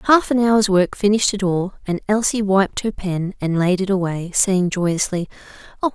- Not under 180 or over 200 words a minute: Yes, average, 190 wpm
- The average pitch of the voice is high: Yes, high, 195 Hz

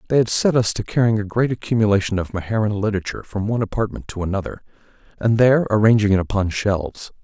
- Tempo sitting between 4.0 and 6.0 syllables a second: No, 7.0 syllables/s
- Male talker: Yes, male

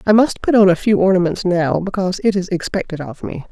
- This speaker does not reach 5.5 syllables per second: No, 6.0 syllables/s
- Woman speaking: Yes, female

